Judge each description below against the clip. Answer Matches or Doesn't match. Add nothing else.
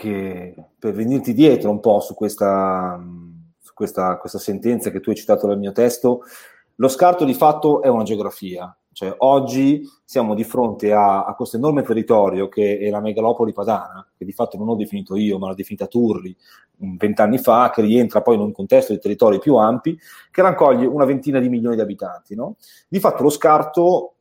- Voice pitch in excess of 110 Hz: Doesn't match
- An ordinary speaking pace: Doesn't match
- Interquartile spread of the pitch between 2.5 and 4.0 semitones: Doesn't match